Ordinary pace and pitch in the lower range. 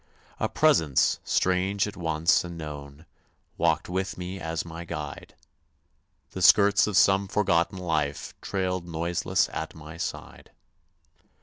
No: slow, 125 wpm; very low, 85 Hz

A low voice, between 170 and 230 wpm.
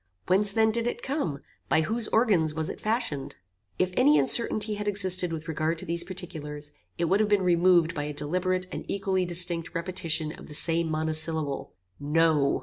No: medium, 170 Hz; average, 180 wpm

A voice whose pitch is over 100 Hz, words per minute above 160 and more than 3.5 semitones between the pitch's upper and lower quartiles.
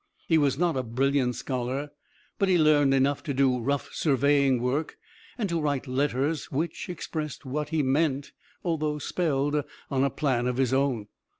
No: medium, 140 Hz; average, 170 wpm; narrow, 2.5 semitones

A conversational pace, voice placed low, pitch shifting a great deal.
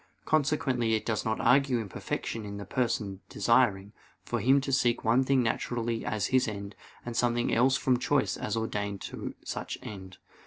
No: average, 170 wpm; low, 115 Hz; average, 3.7 semitones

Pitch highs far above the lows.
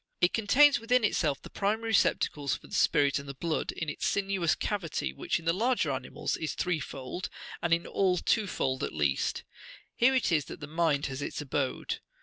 Yes: wide, 6.0 semitones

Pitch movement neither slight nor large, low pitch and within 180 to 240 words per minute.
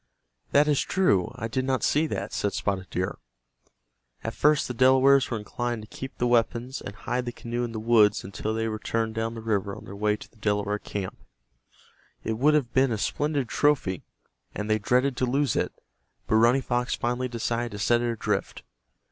Yes: average, 3.2 semitones; low, 120 Hz; average, 200 wpm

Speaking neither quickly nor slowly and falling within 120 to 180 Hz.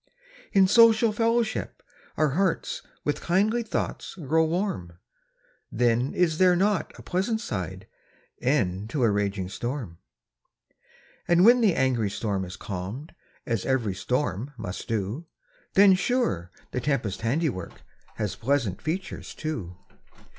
No: slow, 125 wpm; low, 135 Hz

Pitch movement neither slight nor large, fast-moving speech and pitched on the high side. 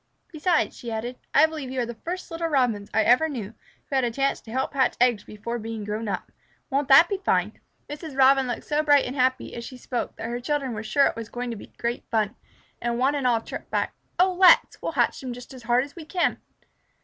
Yes: average, 3.7 semitones; fast, 245 wpm; very high, 255 Hz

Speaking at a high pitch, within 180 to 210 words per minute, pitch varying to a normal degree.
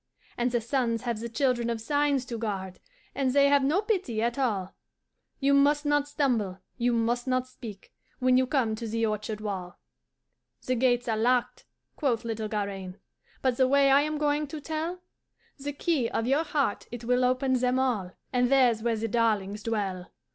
Yes: high, 245 Hz; average, 185 wpm; average, 3.7 semitones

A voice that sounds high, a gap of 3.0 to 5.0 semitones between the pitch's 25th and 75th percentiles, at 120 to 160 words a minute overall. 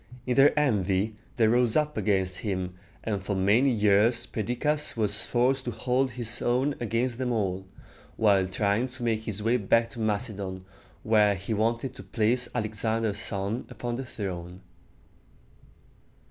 No: low, 110 Hz; average, 3.4 semitones; average, 150 wpm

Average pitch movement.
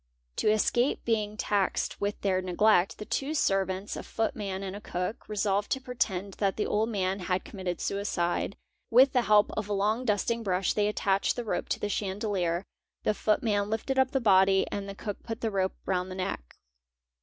No: narrow, 2.3 semitones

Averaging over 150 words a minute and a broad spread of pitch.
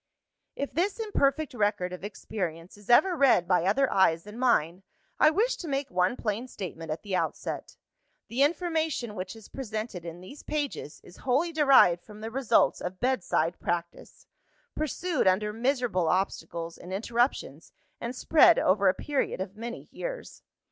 Yes: average, 160 wpm; wide, 7.2 semitones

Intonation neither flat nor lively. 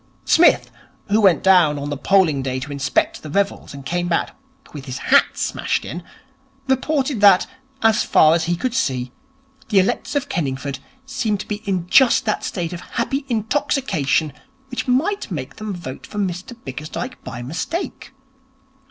No: wide, 8.4 semitones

